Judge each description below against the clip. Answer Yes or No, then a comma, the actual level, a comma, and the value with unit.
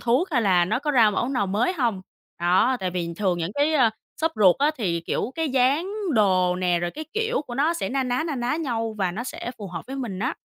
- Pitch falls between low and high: No, high, 235 Hz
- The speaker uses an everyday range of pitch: No, wide, 6.8 semitones